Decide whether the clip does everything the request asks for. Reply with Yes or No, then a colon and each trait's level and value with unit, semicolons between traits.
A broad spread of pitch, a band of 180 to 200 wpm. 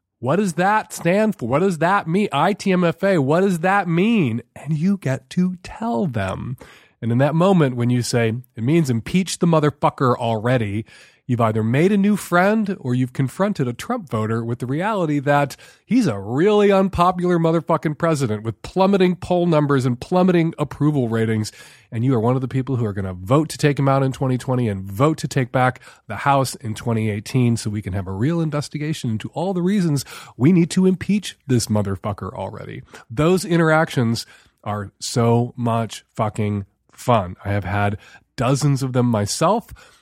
Yes: wide, 7.0 semitones; average, 185 wpm